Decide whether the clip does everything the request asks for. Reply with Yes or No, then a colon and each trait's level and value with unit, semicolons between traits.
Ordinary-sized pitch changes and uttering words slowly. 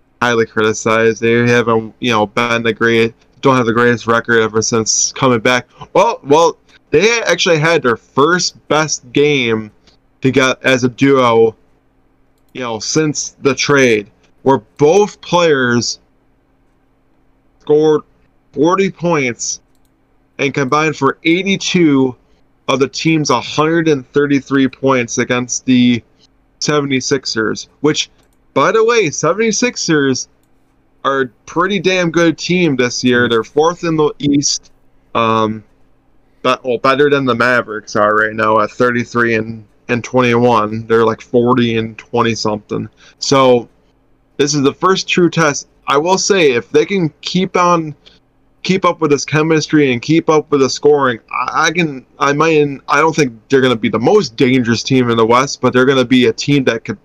No: average, 4.8 semitones; average, 160 wpm